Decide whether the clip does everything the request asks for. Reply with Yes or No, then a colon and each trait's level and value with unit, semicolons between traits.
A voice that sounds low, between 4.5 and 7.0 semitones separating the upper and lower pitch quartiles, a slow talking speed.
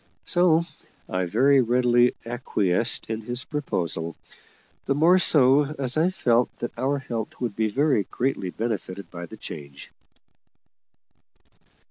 Yes: low, 120 Hz; average, 5.1 semitones; slow, 125 wpm